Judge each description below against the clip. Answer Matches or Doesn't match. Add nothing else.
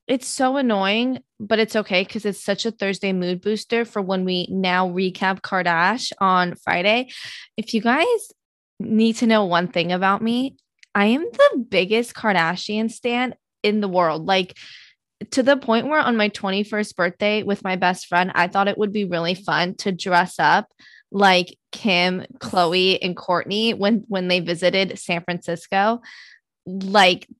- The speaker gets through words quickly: Doesn't match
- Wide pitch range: Doesn't match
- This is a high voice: Matches